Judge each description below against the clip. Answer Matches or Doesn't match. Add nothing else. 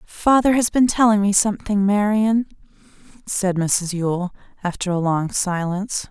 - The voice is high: Matches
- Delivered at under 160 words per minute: Matches